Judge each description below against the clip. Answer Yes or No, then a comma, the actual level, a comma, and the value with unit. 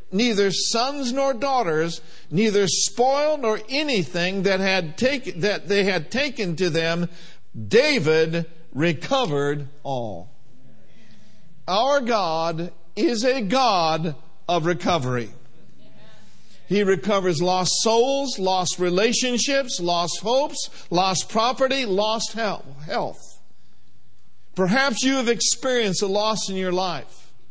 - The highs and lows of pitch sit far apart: Yes, wide, 6.1 semitones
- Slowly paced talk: Yes, slow, 105 wpm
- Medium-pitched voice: No, high, 195 Hz